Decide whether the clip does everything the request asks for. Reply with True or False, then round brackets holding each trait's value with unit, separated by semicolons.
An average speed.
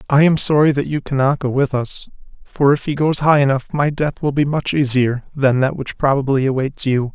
False (225 wpm)